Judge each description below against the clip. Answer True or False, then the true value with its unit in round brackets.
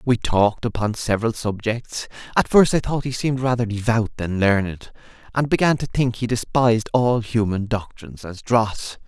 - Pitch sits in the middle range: False (115 Hz)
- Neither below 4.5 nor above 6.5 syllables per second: True (5.1 syllables/s)